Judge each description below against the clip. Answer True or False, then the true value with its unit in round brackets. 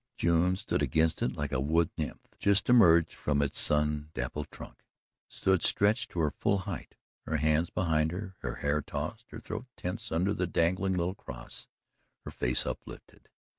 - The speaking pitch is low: True (85 Hz)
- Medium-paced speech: True (170 wpm)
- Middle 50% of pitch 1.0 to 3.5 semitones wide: False (4.2 semitones)